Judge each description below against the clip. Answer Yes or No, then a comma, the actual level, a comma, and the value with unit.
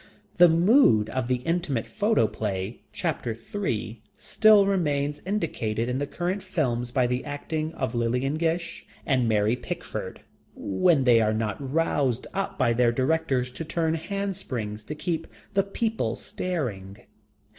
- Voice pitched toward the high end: No, low, 135 Hz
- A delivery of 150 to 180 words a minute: No, average, 140 wpm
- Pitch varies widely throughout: Yes, wide, 6.7 semitones